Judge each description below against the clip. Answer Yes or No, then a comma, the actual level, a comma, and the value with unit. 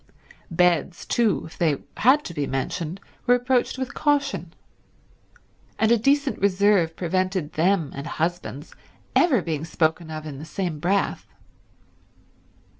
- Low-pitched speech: No, medium, 180 Hz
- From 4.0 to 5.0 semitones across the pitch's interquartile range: No, wide, 5.6 semitones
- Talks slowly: Yes, slow, 130 wpm